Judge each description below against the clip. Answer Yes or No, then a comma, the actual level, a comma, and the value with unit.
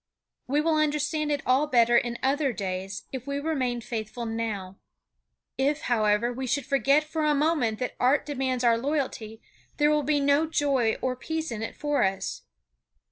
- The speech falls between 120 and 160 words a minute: No, average, 175 wpm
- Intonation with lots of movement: No, average, 4.3 semitones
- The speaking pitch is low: No, very high, 265 Hz